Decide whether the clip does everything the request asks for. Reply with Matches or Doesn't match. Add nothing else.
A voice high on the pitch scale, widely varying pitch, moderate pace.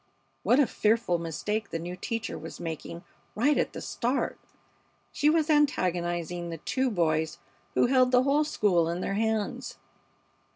Matches